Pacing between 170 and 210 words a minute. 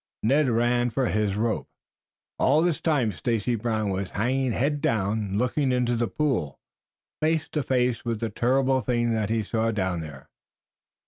No: average, 160 wpm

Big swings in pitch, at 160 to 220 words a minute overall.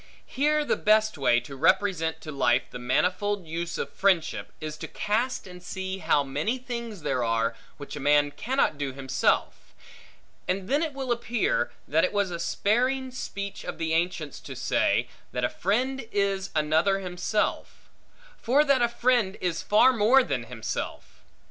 Yes: wide, 7.7 semitones; average, 165 wpm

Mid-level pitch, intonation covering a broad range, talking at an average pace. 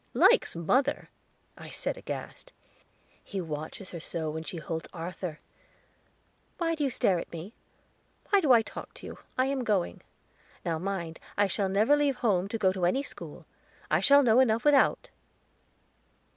No: high, 200 Hz; wide, 7.7 semitones; average, 165 wpm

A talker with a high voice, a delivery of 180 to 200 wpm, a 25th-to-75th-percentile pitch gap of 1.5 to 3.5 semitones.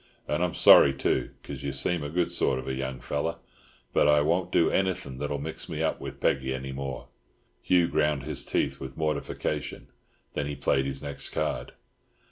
No: very low, 70 Hz; average, 185 wpm; average, 3.0 semitones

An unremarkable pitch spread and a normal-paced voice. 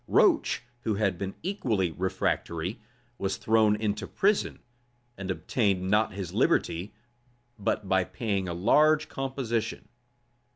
No: average, 3.2 semitones; slow, 120 wpm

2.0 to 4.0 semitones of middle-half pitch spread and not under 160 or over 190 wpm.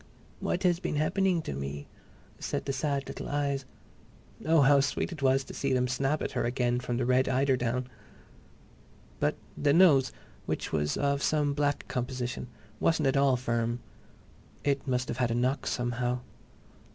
Yes: narrow, 2.6 semitones; average, 165 wpm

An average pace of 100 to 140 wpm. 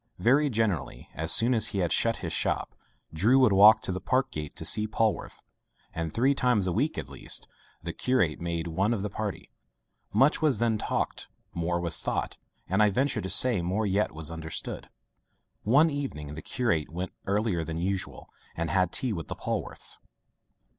No: average, 185 wpm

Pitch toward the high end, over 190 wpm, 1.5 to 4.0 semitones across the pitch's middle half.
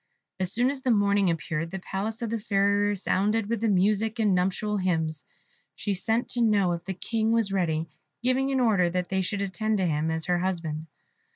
Yes: high, 200 Hz; average, 200 wpm; average, 3.7 semitones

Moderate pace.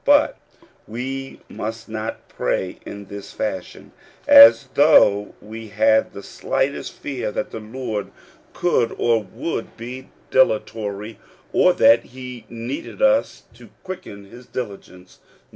No: slow, 125 wpm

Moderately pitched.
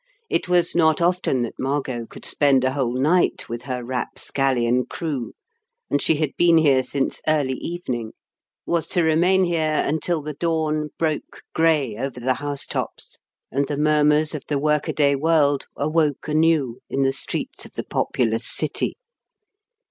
Yes: medium, 145 Hz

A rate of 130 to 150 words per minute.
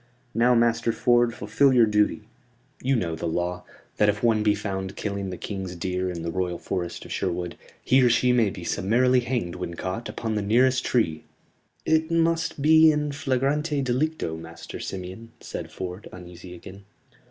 No: average, 175 wpm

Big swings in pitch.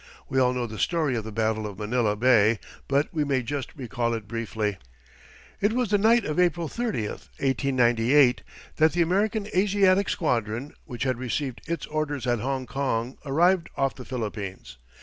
Yes: wide, 5.9 semitones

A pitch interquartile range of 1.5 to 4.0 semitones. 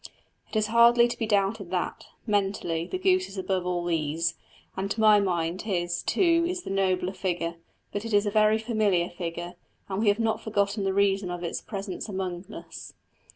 Yes: average, 3.5 semitones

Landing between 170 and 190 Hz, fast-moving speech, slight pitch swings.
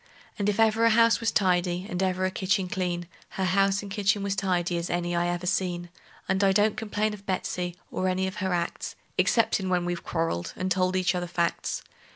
Yes: medium, 185 Hz; fast, 210 wpm; narrow, 2.1 semitones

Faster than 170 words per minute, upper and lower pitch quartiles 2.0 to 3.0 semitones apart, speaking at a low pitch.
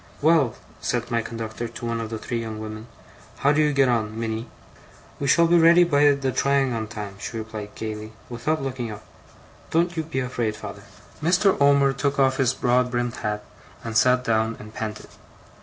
No: average, 190 wpm; average, 4.0 semitones; low, 120 Hz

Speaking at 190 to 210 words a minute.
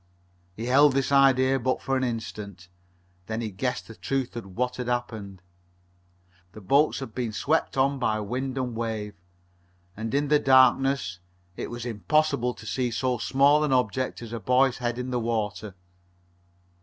No: average, 170 wpm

